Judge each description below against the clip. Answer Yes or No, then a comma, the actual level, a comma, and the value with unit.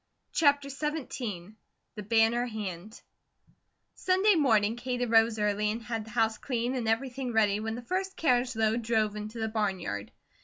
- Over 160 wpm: No, average, 155 wpm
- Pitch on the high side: Yes, high, 225 Hz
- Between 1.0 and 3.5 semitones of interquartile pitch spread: Yes, average, 2.8 semitones